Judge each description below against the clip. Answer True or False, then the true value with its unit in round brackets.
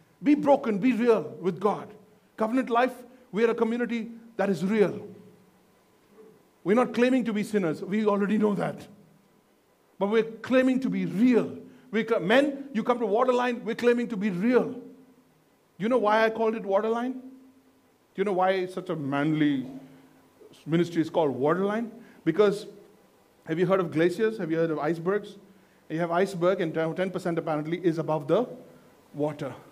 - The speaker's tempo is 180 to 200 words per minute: False (165 wpm)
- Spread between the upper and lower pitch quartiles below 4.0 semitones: False (4.5 semitones)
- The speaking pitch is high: True (210 Hz)